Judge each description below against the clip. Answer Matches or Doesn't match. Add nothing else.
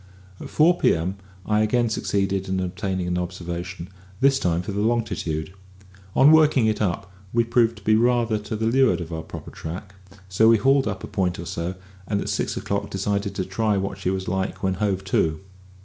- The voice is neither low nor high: Doesn't match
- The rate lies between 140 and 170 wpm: Doesn't match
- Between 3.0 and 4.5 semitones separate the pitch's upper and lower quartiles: Matches